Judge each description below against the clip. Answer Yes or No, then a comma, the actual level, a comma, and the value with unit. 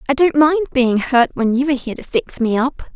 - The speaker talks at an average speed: No, fast, 265 wpm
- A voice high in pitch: Yes, very high, 265 Hz